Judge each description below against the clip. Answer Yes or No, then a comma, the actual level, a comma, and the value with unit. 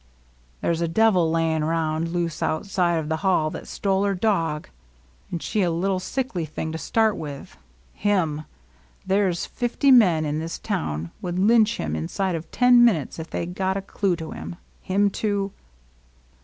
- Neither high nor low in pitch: Yes, medium, 175 Hz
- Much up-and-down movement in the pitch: No, average, 3.9 semitones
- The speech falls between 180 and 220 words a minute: Yes, average, 185 wpm